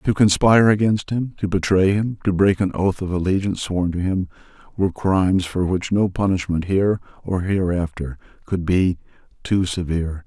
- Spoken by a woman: No, male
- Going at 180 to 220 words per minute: No, average, 170 wpm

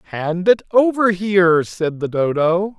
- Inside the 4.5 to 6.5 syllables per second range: No, 3.8 syllables/s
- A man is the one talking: Yes, male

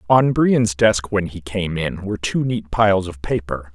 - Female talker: No, male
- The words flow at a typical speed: No, fast, 210 wpm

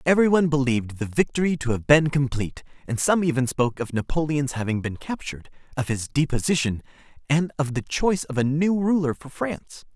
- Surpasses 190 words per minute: No, average, 180 wpm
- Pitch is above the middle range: No, medium, 140 Hz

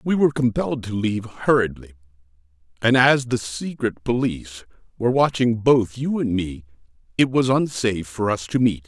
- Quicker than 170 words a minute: No, average, 160 wpm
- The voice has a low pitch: Yes, low, 115 Hz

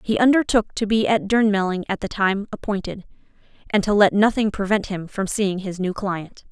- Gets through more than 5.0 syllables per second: Yes, 5.3 syllables/s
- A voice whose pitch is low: No, high, 200 Hz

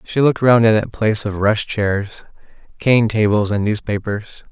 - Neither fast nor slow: Yes, average, 160 wpm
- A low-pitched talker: Yes, low, 110 Hz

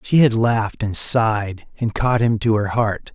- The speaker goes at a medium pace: No, fast, 210 wpm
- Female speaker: No, male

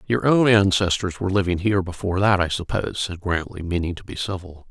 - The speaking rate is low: No, fast, 205 wpm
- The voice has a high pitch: No, very low, 95 Hz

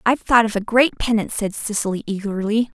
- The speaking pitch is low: No, high, 215 Hz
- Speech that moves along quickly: No, average, 195 wpm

